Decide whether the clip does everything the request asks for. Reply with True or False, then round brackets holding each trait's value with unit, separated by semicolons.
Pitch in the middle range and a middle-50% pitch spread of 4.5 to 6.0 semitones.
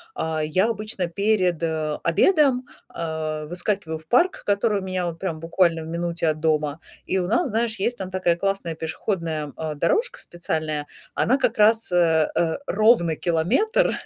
True (175 Hz; 4.8 semitones)